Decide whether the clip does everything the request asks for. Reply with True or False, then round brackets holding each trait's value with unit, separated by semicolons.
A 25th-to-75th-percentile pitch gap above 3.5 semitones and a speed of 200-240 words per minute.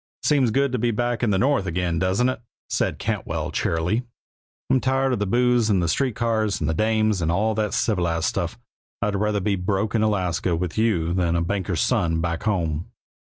True (4.8 semitones; 205 wpm)